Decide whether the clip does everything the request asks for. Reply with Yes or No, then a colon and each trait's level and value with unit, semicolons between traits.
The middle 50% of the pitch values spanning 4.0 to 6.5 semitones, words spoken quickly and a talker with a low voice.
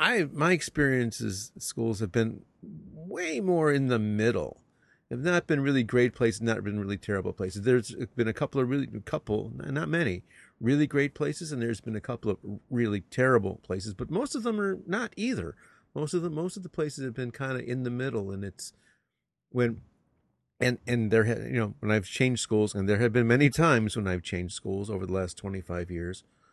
Yes: average, 5.1 semitones; fast, 210 wpm; low, 120 Hz